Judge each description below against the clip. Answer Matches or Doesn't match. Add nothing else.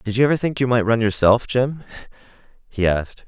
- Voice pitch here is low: Matches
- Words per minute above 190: Matches